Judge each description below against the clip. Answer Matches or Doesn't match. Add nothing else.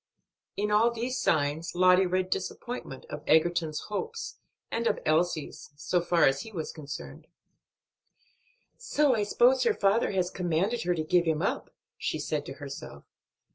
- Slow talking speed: Doesn't match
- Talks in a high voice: Doesn't match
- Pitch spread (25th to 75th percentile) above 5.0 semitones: Matches